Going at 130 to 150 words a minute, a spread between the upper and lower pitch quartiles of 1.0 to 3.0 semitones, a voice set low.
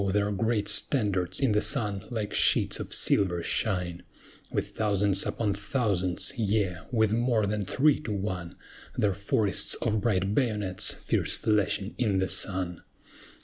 Yes: average, 145 wpm; narrow, 2.5 semitones; low, 105 Hz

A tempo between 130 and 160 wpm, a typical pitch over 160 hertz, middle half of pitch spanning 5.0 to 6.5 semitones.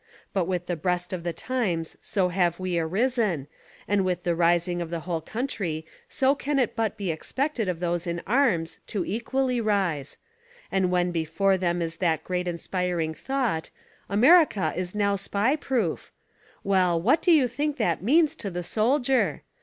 No: average, 175 wpm; medium, 185 Hz; wide, 5.5 semitones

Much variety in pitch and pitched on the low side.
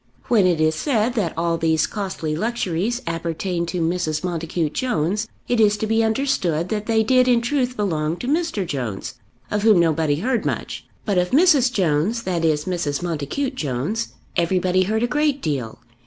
No: wide, 6.2 semitones; medium, 185 Hz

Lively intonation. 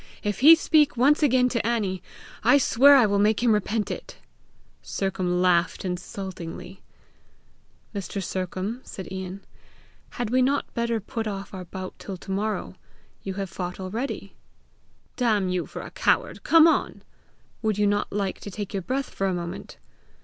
No: average, 4.0 semitones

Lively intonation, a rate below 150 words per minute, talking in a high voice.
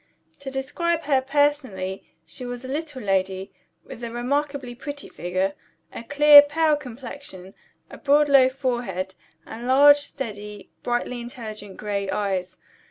Yes: wide, 5.8 semitones; slow, 135 wpm; very high, 250 Hz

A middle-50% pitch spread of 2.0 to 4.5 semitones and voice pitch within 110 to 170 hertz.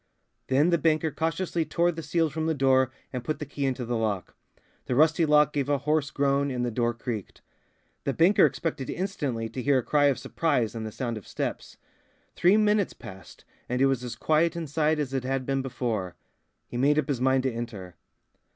Yes: average, 4.1 semitones; medium, 140 Hz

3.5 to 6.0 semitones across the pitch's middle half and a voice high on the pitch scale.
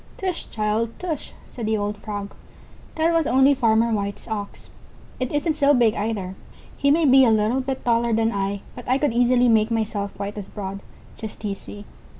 Yes: average, 4.2 semitones; high, 225 Hz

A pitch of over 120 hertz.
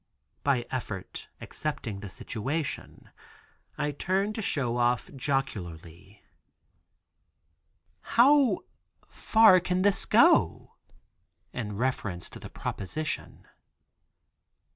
Yes: low, 135 Hz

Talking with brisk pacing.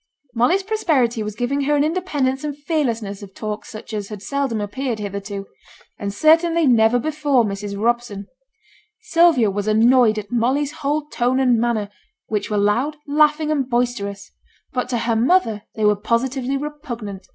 No: average, 160 wpm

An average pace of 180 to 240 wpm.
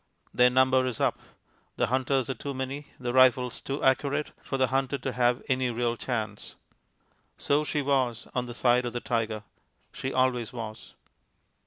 No: average, 170 wpm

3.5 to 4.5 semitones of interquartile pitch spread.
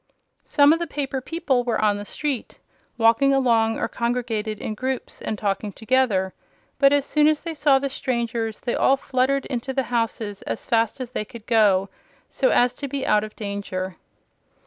Yes: average, 4.1 semitones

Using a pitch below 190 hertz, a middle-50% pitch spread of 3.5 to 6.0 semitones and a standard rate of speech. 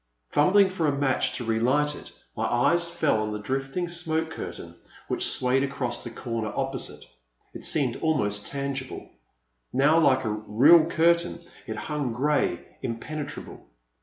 Yes: medium, 140 Hz; average, 4.7 semitones; average, 145 wpm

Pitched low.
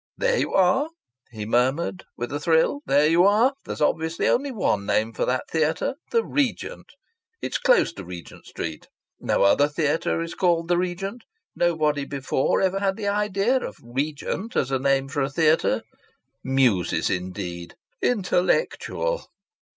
No: medium, 160 Hz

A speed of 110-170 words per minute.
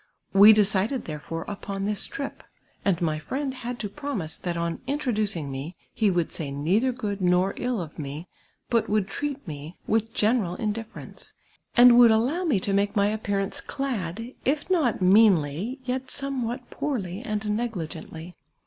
Yes: average, 160 wpm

